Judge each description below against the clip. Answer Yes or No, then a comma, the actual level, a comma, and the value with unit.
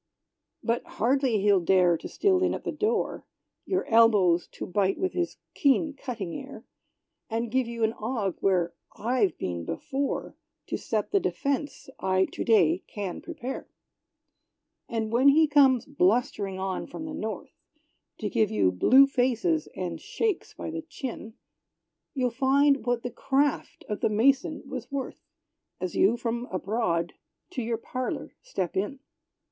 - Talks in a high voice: Yes, high, 235 Hz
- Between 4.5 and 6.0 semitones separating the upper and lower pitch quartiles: Yes, wide, 5.5 semitones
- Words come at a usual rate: Yes, average, 150 wpm